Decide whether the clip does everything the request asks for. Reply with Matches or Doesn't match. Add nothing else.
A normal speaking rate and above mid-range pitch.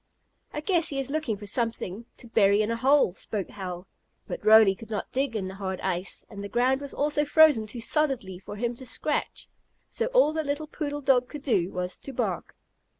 Doesn't match